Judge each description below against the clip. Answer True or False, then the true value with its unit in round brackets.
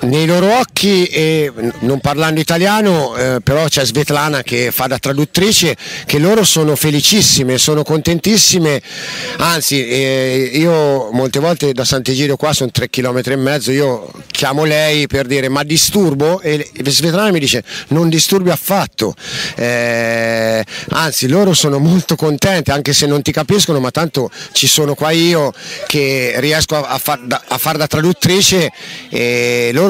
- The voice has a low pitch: False (150 Hz)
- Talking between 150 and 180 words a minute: True (155 wpm)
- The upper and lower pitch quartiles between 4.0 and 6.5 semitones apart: False (3.5 semitones)